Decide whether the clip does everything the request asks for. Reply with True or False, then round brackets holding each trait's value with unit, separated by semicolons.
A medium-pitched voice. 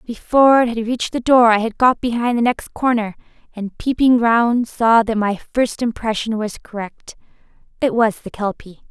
False (230 Hz)